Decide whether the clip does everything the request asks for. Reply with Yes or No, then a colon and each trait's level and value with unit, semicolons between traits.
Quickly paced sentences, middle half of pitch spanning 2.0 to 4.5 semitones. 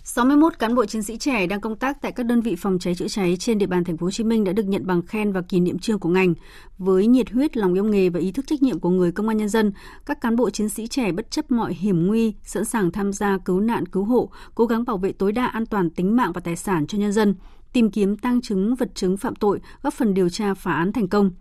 Yes: fast, 290 wpm; average, 3.8 semitones